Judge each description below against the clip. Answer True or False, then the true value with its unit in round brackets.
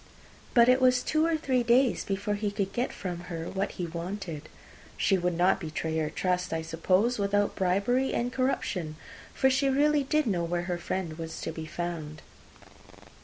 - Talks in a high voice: True (195 Hz)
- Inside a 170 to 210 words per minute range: True (180 wpm)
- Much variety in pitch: True (6.4 semitones)